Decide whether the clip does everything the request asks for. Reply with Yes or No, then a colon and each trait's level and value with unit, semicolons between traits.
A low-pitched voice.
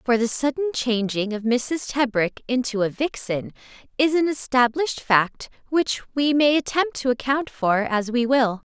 No: very high, 255 Hz